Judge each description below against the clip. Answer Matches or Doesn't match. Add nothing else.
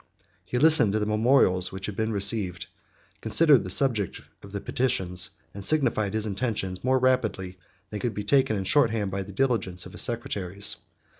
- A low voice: Matches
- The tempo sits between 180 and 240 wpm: Matches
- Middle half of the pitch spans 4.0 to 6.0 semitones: Matches